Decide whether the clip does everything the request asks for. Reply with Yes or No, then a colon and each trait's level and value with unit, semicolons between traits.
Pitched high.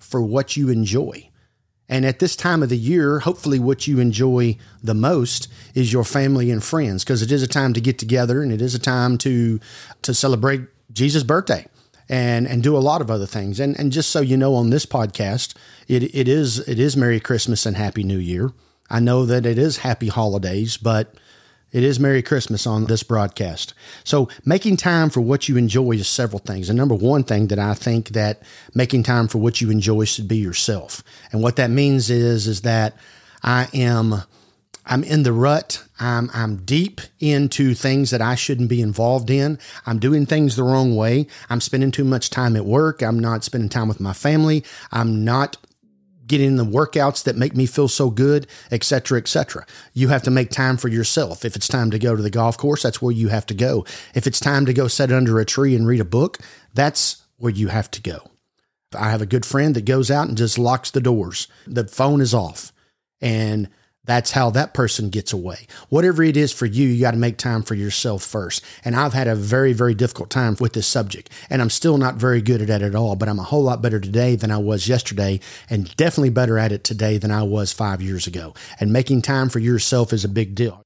No: low, 120 Hz